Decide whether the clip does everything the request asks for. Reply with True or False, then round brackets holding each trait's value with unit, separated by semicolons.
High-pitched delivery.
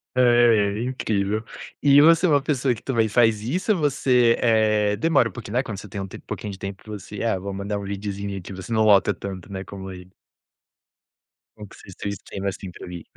False (105 Hz)